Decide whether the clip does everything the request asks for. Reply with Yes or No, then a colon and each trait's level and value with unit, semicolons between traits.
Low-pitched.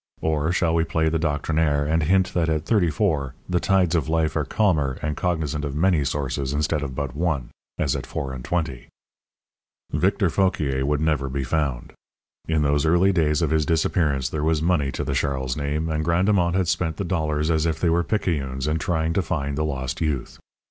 Yes: very low, 80 Hz